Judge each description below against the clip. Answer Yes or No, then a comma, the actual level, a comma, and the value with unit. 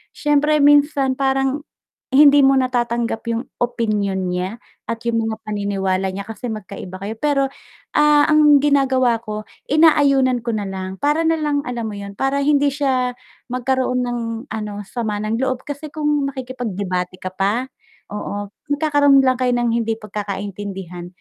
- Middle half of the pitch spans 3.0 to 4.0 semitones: No, average, 5.3 semitones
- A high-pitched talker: Yes, high, 245 Hz